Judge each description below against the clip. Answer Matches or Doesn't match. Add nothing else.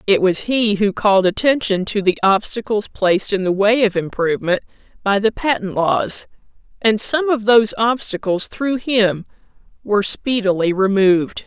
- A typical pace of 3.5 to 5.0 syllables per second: Matches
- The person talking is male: Doesn't match